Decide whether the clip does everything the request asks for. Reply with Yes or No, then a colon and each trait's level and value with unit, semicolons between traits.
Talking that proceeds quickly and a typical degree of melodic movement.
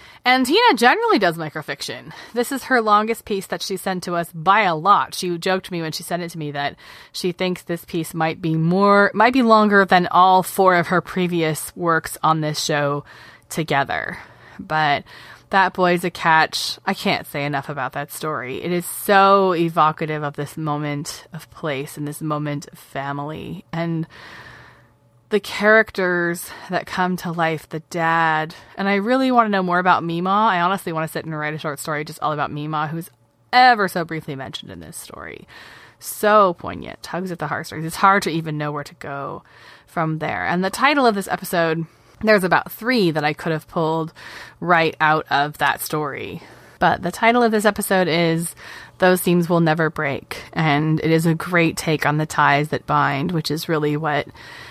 No: average, 195 wpm; average, 3.6 semitones